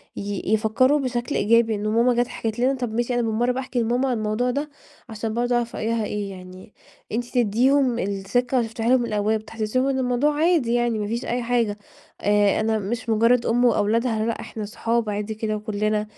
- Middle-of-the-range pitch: No, high, 230 Hz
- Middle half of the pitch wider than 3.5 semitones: No, narrow, 2.4 semitones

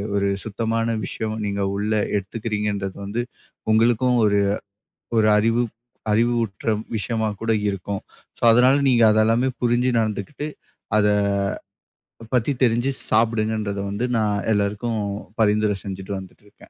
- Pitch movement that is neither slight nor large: No, narrow, 2.3 semitones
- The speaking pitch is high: No, low, 110 Hz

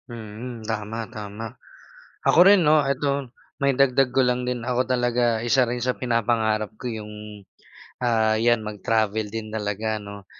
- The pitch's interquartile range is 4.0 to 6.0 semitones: No, narrow, 2.5 semitones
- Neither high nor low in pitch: No, low, 115 Hz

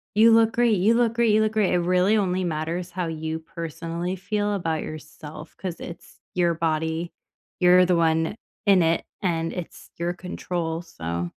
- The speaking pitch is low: No, medium, 175 Hz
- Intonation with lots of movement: No, average, 2.7 semitones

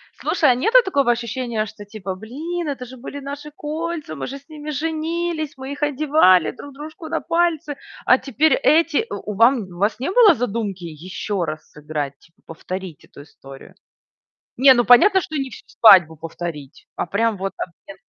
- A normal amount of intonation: No, wide, 8.3 semitones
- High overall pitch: Yes, very high, 255 Hz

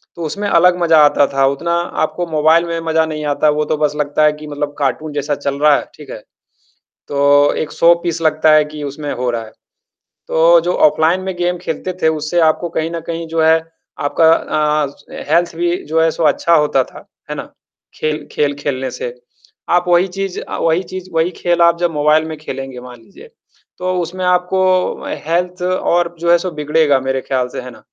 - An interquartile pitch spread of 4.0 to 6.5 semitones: No, average, 2.7 semitones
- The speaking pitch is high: No, medium, 160 Hz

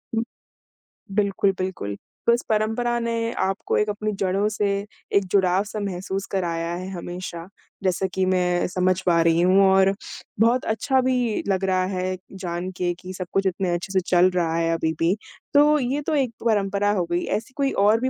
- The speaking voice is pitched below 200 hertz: Yes, high, 190 Hz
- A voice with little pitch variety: No, average, 3.2 semitones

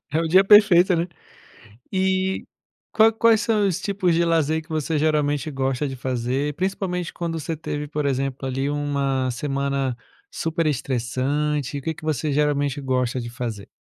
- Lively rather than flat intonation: No, average, 4.1 semitones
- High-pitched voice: No, medium, 150 Hz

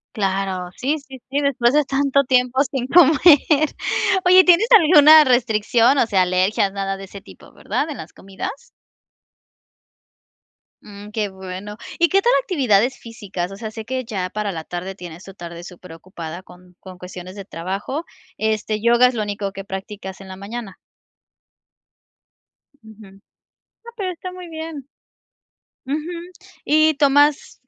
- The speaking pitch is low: No, high, 220 Hz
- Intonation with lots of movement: Yes, wide, 6.7 semitones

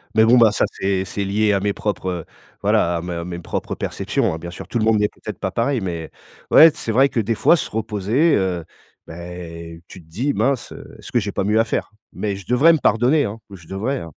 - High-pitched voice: No, low, 105 Hz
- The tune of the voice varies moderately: Yes, average, 4.1 semitones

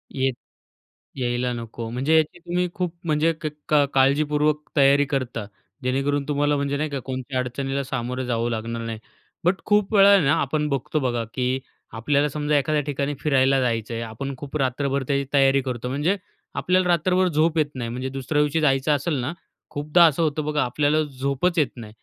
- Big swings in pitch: No, average, 2.9 semitones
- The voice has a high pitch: No, medium, 140 Hz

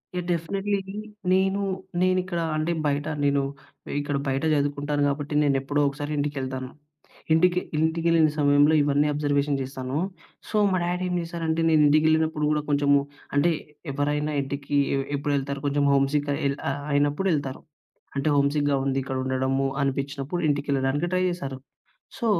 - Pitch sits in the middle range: Yes, medium, 145 Hz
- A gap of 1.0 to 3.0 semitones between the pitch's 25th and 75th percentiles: Yes, narrow, 2.4 semitones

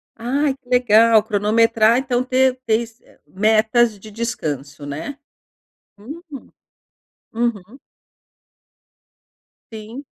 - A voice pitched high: Yes, high, 230 Hz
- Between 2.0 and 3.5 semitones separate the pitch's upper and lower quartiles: Yes, average, 2.8 semitones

